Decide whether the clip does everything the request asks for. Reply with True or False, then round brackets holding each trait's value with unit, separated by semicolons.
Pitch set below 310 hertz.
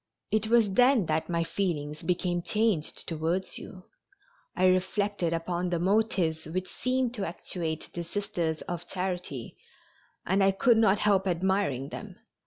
True (185 Hz)